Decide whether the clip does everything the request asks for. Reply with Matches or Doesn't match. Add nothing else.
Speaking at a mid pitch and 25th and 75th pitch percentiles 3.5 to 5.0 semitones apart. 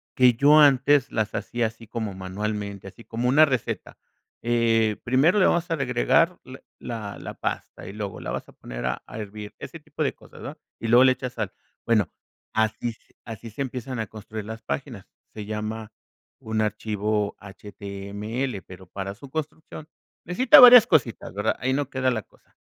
Doesn't match